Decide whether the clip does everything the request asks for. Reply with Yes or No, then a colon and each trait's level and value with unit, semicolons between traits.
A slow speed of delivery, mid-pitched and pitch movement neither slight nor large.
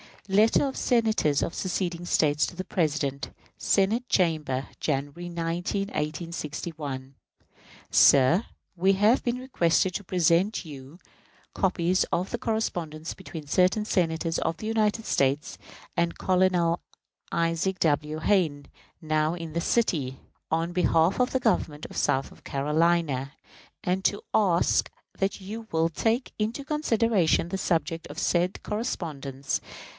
Yes: slow, 130 wpm; medium, 170 Hz; average, 4.3 semitones